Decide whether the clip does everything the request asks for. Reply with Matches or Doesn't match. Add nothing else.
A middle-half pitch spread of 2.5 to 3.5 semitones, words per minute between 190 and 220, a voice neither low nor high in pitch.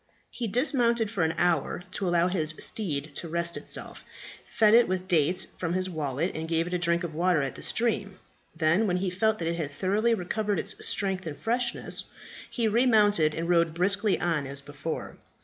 Doesn't match